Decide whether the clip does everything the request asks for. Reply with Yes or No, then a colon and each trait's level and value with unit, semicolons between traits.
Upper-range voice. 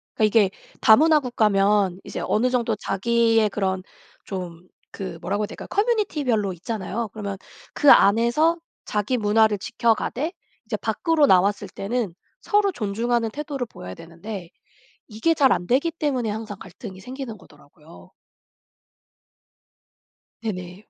Yes: high, 220 Hz